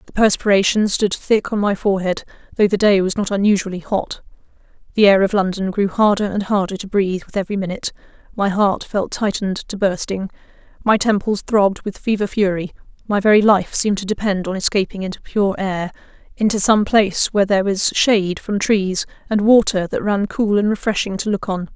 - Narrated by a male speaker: No, female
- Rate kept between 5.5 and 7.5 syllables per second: Yes, 5.8 syllables/s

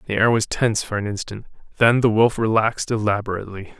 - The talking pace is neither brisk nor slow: Yes, average, 190 wpm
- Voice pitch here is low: Yes, low, 110 Hz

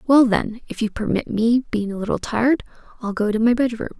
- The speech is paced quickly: Yes, fast, 240 wpm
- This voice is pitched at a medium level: No, high, 230 Hz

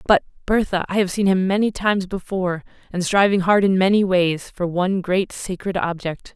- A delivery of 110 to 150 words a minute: No, average, 190 wpm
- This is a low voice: No, medium, 185 Hz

